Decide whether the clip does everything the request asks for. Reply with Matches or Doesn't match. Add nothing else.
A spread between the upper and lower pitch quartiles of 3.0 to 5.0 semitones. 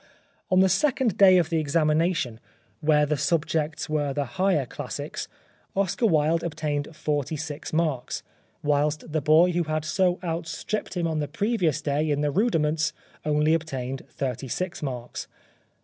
Doesn't match